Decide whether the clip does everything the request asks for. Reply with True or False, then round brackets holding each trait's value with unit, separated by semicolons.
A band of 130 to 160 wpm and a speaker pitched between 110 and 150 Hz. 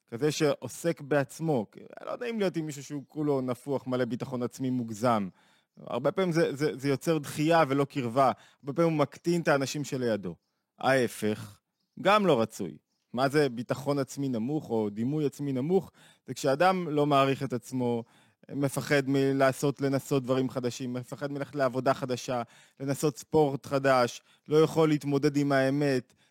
True (150 wpm; 140 Hz)